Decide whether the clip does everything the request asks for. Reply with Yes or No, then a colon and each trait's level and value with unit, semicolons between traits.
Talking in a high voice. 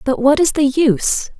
Yes: very high, 280 Hz